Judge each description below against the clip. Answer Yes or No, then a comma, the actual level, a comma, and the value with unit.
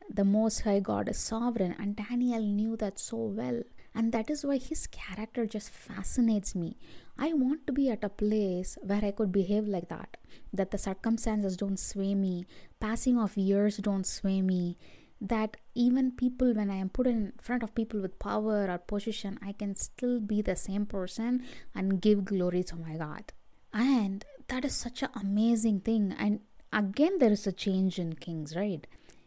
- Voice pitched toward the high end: Yes, high, 210 Hz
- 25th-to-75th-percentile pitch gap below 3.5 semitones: Yes, average, 3.1 semitones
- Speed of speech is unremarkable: Yes, average, 185 wpm